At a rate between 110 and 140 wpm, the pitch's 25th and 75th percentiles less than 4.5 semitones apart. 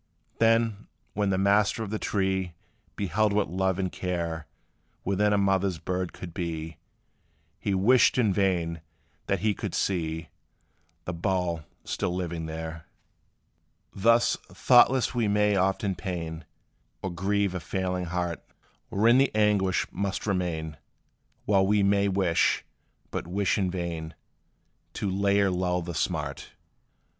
Yes: slow, 135 wpm; average, 2.8 semitones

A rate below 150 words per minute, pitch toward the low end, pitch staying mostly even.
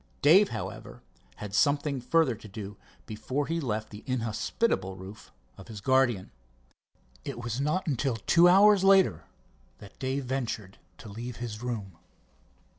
No: average, 140 wpm; low, 120 Hz; average, 5.2 semitones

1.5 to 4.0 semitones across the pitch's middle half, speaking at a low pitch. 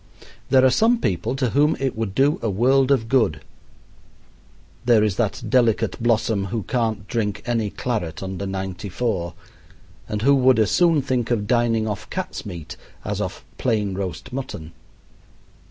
No: average, 4.5 semitones; low, 115 Hz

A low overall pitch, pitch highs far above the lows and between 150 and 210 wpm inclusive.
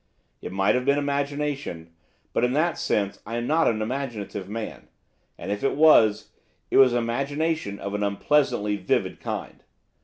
Yes: low, 120 Hz; wide, 5.7 semitones; average, 160 wpm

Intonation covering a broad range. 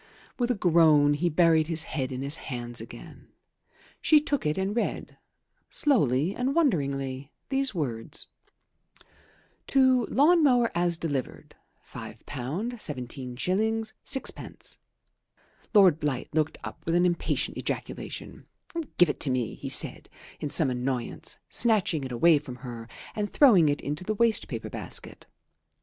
Yes: wide, 8.2 semitones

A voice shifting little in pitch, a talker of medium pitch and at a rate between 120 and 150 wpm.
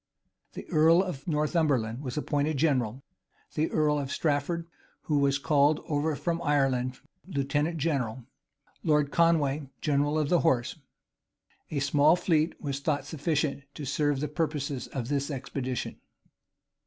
Yes: narrow, 2.3 semitones; medium, 145 Hz; average, 140 wpm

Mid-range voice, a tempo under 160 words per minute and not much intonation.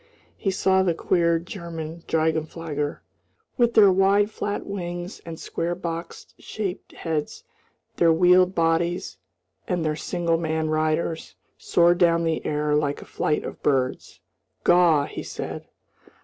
Yes: medium, 170 Hz; slow, 135 wpm; narrow, 2.2 semitones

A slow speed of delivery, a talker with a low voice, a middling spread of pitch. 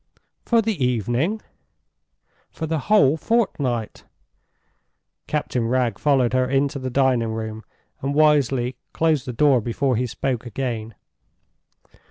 Yes: slow, 120 wpm; low, 130 Hz; average, 3.7 semitones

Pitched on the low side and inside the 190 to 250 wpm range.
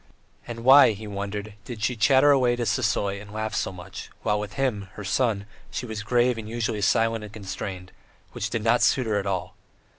Yes: low, 110 Hz; fast, 205 wpm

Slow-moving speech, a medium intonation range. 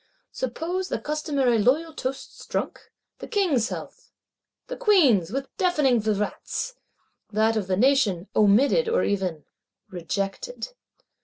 No: slow, 110 wpm; wide, 7.9 semitones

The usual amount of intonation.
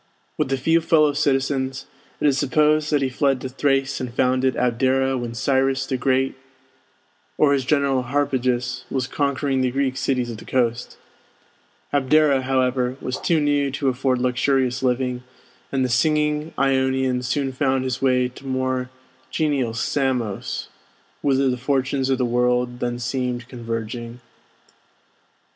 No: narrow, 1.6 semitones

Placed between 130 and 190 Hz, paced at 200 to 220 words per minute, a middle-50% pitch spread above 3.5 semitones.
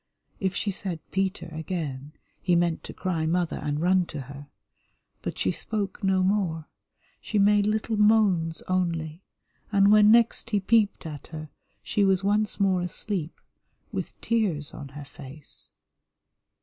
No: medium, 185 Hz; average, 150 wpm; average, 4.3 semitones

